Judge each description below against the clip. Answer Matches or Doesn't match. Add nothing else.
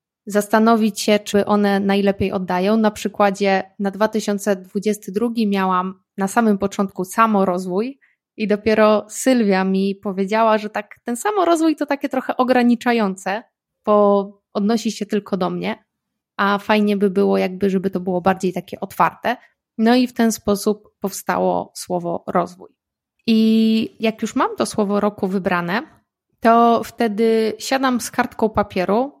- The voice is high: Matches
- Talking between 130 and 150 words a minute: Matches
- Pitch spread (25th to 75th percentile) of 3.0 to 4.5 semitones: Doesn't match